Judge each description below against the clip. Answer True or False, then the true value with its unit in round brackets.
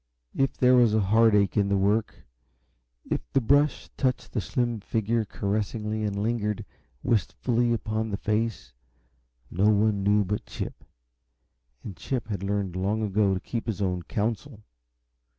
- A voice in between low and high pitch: False (105 Hz)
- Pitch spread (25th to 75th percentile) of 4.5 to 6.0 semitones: False (2.4 semitones)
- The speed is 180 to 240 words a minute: False (150 wpm)